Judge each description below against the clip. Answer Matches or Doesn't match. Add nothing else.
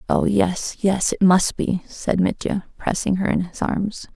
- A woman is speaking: Matches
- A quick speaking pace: Doesn't match